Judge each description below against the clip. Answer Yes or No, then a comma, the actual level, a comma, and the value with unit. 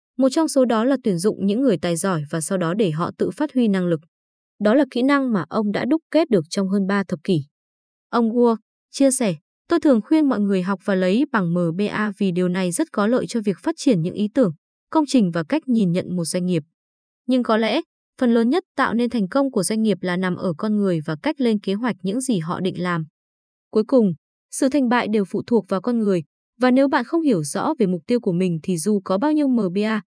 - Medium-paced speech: No, fast, 255 wpm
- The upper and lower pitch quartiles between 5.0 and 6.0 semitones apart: Yes, wide, 5.5 semitones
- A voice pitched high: Yes, high, 215 Hz